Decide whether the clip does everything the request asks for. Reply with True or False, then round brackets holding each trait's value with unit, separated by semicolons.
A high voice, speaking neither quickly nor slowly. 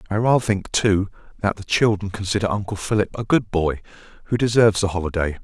False (100 Hz; 190 wpm)